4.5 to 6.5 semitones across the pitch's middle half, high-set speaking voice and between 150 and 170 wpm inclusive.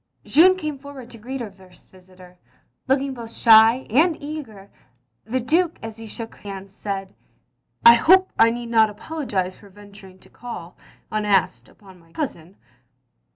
Yes: wide, 5.5 semitones; high, 225 Hz; average, 160 wpm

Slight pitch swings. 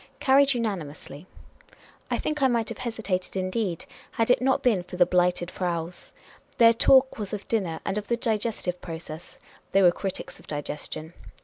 No: average, 4.8 semitones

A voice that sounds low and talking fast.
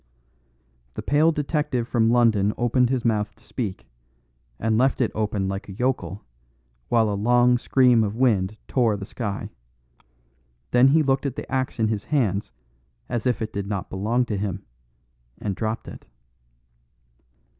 No: low, 115 Hz; average, 155 wpm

